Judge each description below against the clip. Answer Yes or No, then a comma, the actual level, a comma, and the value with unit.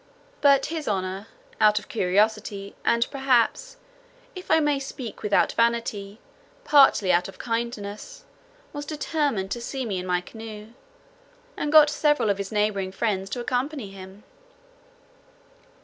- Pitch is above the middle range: Yes, high, 225 Hz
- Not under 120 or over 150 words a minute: Yes, slow, 135 wpm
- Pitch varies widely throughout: Yes, wide, 5.7 semitones